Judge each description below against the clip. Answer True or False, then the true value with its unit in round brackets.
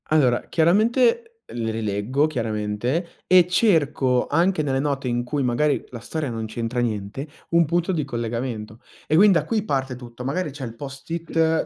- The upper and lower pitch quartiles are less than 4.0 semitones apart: False (5.6 semitones)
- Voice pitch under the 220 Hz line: True (135 Hz)